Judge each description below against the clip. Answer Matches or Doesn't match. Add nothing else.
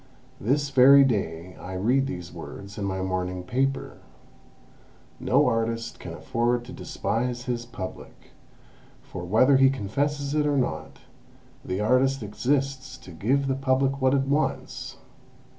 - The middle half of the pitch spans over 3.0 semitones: Matches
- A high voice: Doesn't match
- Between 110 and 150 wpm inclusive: Matches